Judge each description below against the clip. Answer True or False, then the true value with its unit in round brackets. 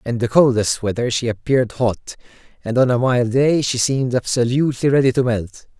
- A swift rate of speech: False (185 wpm)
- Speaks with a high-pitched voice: False (120 Hz)